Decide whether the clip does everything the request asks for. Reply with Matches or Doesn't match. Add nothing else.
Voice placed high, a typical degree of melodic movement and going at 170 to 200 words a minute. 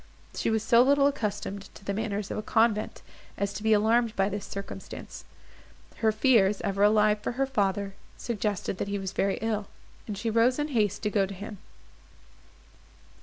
Doesn't match